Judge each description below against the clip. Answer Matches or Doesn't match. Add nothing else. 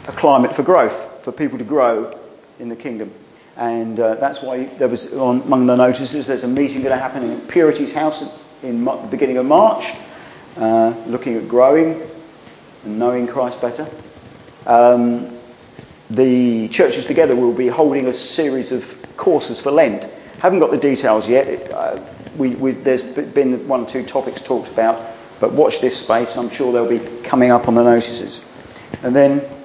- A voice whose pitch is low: Matches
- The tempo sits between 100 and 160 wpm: Doesn't match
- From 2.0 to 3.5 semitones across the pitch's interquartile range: Matches